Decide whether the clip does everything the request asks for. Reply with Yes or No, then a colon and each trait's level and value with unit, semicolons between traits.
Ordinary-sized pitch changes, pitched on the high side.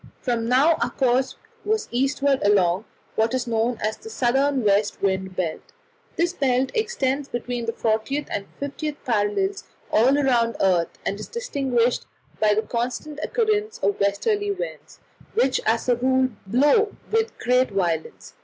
Yes: average, 5.0 semitones; very high, 250 Hz